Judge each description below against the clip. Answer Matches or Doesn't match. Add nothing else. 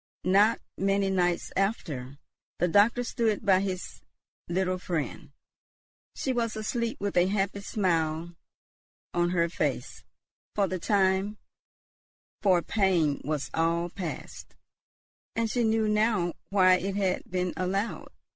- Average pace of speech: Doesn't match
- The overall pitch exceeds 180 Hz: Matches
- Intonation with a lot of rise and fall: Doesn't match